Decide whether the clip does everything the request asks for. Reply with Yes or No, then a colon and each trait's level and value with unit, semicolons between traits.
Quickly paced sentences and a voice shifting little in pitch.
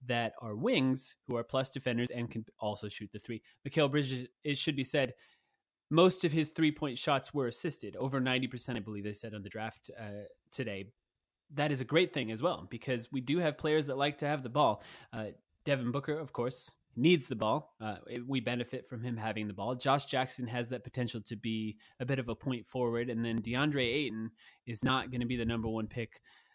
No: fast, 220 wpm; average, 3.5 semitones